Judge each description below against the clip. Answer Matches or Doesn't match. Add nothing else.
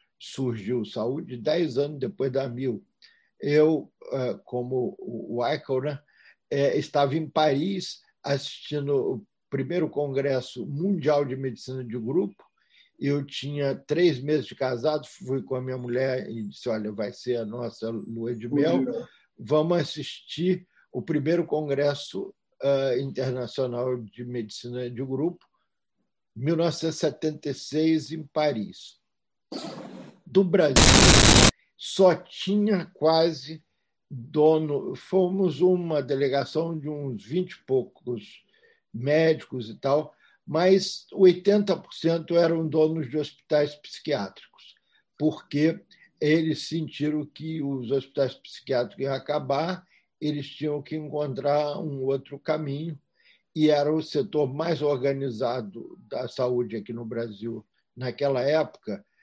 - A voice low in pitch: Doesn't match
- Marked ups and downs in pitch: Doesn't match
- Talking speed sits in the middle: Doesn't match